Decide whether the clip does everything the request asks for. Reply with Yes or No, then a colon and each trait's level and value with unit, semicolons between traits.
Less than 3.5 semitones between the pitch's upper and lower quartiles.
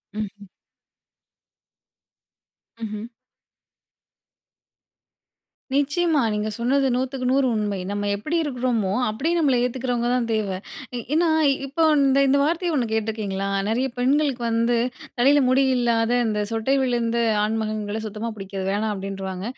No: average, 4.0 semitones